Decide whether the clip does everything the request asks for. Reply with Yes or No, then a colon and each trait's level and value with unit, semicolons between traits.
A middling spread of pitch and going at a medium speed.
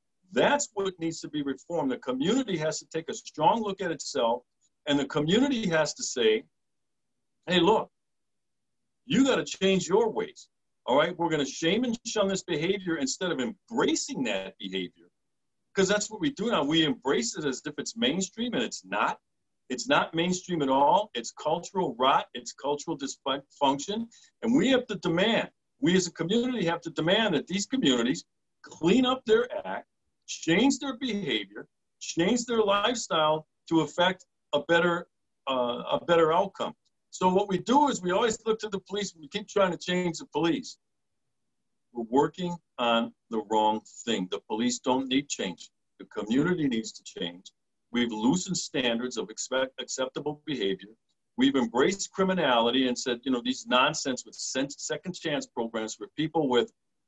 No: wide, 8.0 semitones; average, 170 wpm